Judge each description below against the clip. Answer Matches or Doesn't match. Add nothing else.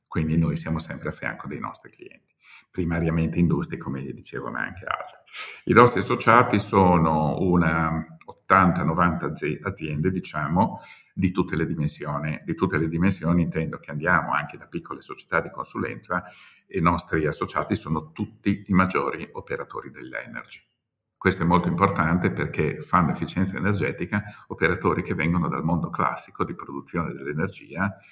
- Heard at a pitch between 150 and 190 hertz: Doesn't match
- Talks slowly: Doesn't match